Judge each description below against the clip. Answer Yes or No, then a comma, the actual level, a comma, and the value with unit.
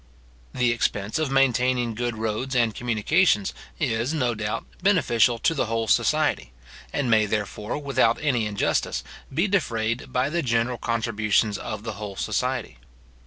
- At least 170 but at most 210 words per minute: No, average, 145 wpm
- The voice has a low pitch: Yes, low, 115 Hz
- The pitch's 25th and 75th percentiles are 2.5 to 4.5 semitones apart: Yes, average, 3.2 semitones